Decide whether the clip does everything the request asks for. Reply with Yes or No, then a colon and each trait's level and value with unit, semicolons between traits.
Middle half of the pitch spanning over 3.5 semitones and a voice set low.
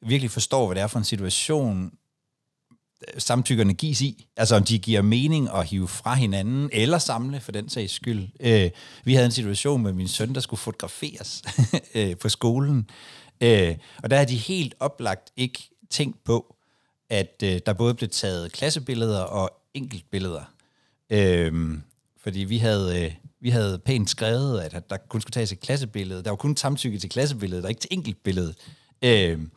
Yes: average, 4.7 semitones; low, 115 Hz